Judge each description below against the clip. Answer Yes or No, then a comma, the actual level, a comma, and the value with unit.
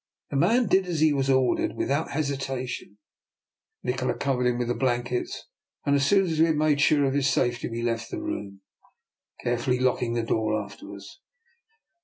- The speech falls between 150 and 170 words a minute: No, average, 180 wpm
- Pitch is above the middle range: No, low, 130 Hz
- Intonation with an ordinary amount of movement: Yes, average, 3.3 semitones